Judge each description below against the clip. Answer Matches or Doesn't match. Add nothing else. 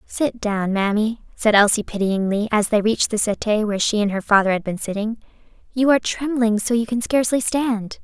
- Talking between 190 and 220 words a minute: Matches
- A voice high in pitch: Matches